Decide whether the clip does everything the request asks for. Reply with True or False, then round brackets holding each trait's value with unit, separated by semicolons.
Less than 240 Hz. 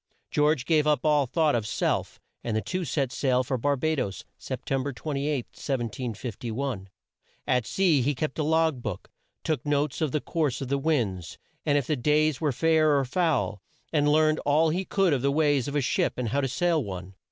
True (140 Hz)